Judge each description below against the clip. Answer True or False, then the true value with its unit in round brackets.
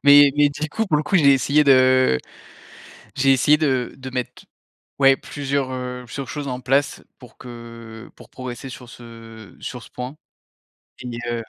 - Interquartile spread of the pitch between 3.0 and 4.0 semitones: False (2.5 semitones)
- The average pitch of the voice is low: True (130 Hz)